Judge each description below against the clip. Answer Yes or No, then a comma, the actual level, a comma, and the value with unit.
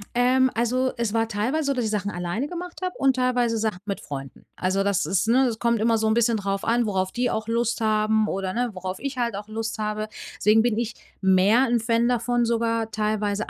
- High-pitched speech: Yes, high, 225 Hz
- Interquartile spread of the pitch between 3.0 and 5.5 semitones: No, narrow, 2.6 semitones